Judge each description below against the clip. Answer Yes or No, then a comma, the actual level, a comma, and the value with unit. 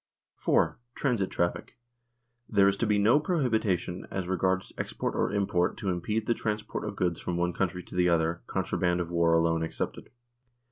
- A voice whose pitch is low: Yes, very low, 95 Hz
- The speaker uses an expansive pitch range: No, average, 3.2 semitones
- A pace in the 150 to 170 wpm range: No, average, 180 wpm